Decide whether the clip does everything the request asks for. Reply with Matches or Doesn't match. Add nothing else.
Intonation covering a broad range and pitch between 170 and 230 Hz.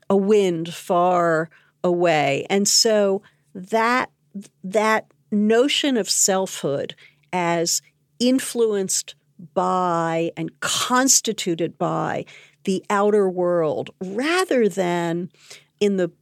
Doesn't match